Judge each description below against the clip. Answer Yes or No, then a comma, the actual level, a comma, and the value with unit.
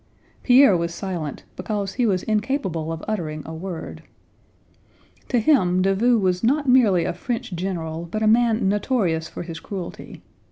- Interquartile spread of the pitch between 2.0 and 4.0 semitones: No, average, 5.2 semitones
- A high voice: Yes, high, 195 Hz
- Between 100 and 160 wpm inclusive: Yes, average, 155 wpm